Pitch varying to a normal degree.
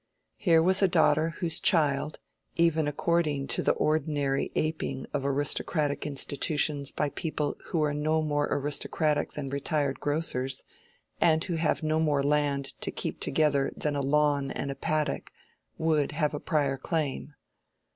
No: narrow, 1.9 semitones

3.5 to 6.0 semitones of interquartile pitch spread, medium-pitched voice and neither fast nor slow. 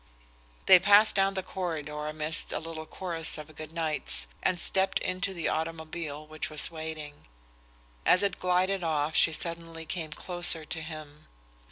No: average, 2.7 semitones; medium, 165 Hz; average, 155 wpm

